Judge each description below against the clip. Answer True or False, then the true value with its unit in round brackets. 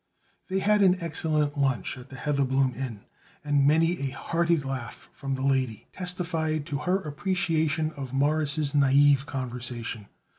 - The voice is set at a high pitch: False (145 Hz)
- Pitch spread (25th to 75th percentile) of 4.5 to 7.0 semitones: False (3.4 semitones)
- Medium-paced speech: True (145 wpm)